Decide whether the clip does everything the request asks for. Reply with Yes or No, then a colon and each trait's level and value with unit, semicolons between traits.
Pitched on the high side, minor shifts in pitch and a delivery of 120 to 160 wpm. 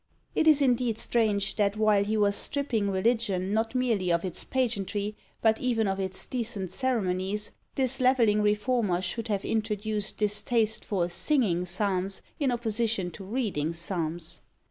No: high, 210 Hz; average, 3.5 semitones; average, 150 wpm